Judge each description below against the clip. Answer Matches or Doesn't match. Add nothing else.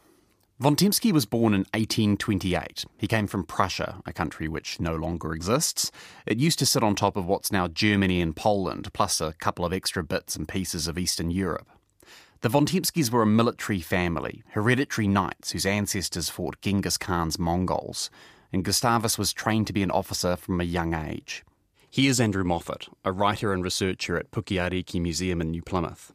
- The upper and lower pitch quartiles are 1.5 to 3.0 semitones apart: Doesn't match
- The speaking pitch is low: Matches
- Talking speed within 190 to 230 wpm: Doesn't match